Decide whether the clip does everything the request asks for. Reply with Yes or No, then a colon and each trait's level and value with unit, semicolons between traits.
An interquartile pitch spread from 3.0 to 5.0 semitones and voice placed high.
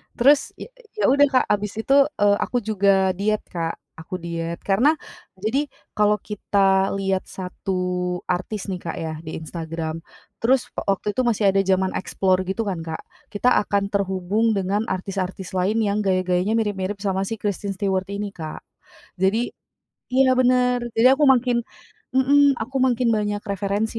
Yes: average, 3.3 semitones; high, 200 Hz